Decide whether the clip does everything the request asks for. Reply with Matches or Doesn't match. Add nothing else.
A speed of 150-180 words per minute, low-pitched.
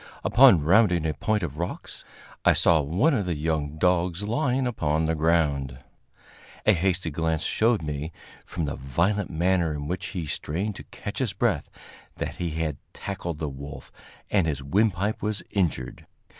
Matches